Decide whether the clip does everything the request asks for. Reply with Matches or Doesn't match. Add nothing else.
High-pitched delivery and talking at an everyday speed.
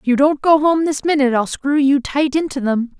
Doesn't match